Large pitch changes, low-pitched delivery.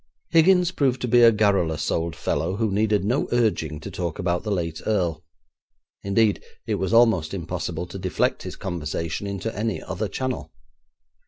No: average, 4.8 semitones; low, 100 Hz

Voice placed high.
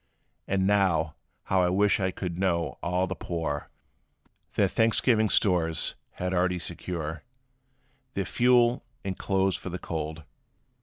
No: very low, 90 Hz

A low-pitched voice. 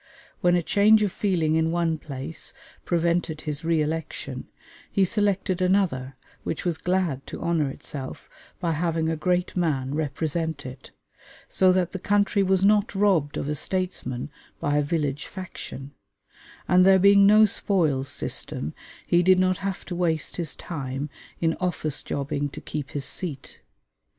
No: medium, 165 Hz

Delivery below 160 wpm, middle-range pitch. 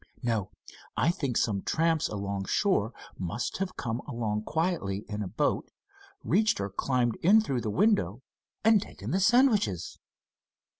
No: average, 145 wpm; low, 120 Hz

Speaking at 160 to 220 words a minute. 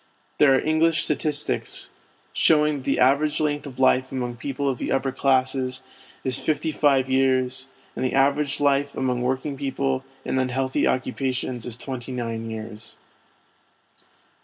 No: average, 150 wpm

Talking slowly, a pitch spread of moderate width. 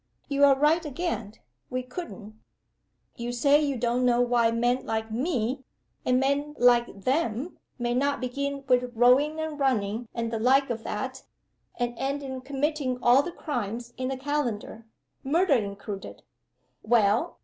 No: average, 150 wpm; average, 3.0 semitones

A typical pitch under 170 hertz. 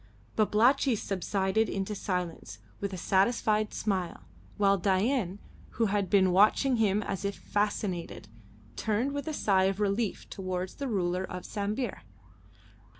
No: high, 200 Hz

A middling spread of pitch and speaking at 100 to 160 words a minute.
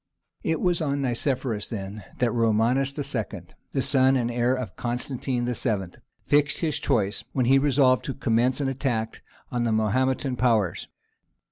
Yes: average, 3.1 semitones; average, 150 wpm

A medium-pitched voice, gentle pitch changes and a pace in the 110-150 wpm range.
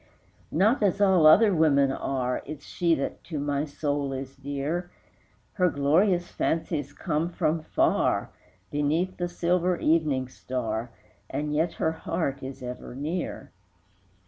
No: medium, 155 Hz; average, 4.0 semitones; slow, 135 wpm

